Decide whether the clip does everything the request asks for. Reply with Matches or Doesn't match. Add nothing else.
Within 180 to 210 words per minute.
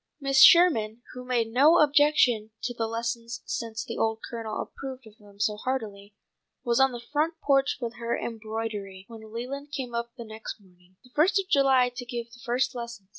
Matches